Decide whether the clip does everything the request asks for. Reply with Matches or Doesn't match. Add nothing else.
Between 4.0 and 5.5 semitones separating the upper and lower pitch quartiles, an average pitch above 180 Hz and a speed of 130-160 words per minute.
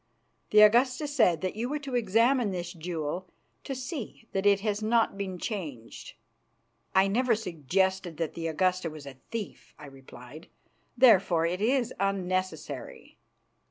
Matches